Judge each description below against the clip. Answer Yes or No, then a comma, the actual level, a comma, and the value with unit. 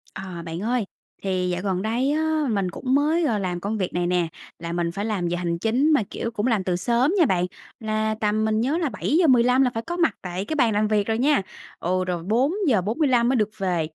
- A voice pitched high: Yes, high, 215 Hz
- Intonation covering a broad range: Yes, wide, 5.9 semitones